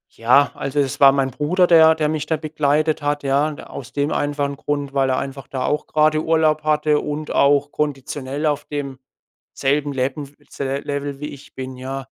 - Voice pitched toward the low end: No, medium, 145 Hz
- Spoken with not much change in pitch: Yes, narrow, 1.8 semitones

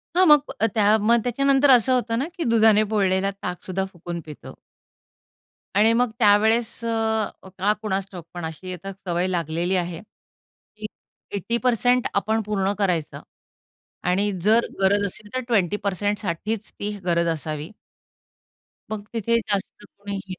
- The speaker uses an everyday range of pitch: Yes, average, 3.4 semitones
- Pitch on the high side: Yes, high, 205 Hz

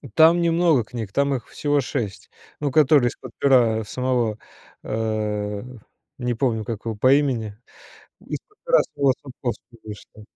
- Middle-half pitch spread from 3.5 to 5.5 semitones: Yes, average, 4.4 semitones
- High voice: No, low, 125 Hz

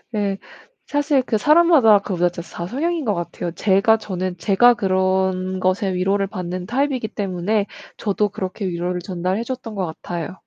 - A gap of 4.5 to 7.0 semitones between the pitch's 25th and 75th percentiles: No, average, 3.3 semitones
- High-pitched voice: Yes, high, 195 Hz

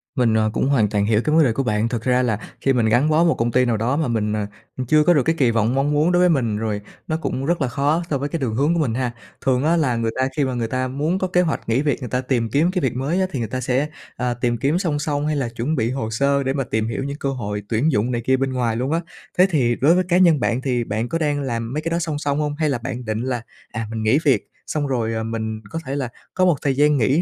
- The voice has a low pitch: Yes, low, 130 Hz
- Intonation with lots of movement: No, average, 4.3 semitones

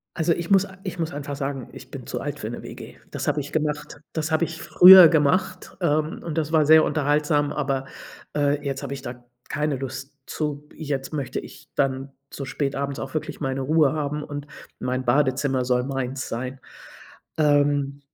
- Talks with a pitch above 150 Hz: No, medium, 145 Hz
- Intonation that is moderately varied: No, narrow, 2.3 semitones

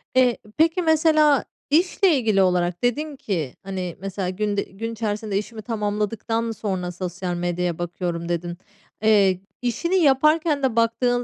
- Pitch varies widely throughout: Yes, wide, 6.1 semitones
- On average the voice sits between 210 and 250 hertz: Yes, high, 215 Hz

